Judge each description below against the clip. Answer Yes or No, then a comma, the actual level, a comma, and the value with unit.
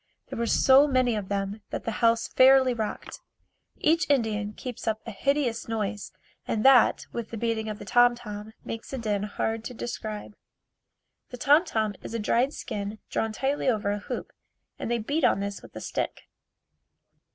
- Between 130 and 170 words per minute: No, average, 185 wpm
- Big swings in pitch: No, average, 3.0 semitones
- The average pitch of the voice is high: Yes, high, 225 Hz